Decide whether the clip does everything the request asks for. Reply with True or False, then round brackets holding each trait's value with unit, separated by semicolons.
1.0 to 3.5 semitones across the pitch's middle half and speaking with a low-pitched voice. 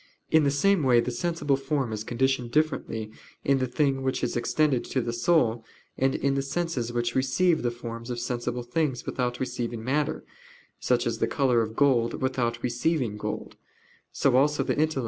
True (2.9 semitones; 130 Hz)